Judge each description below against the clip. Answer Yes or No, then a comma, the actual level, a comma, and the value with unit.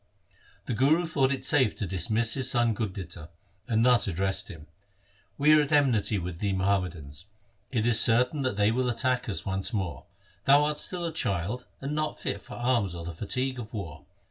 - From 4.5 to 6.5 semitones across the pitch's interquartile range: Yes, average, 5.3 semitones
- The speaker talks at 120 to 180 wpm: No, average, 195 wpm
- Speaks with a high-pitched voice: No, low, 115 Hz